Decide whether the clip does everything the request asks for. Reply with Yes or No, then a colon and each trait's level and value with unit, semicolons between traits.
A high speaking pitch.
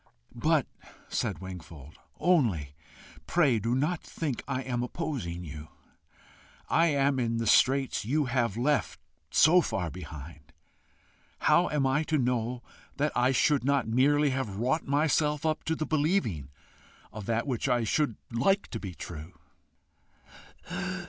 No: low, 125 Hz